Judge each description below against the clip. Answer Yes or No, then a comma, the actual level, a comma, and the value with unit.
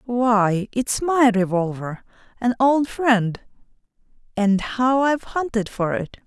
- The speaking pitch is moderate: No, high, 230 Hz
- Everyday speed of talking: No, slow, 125 wpm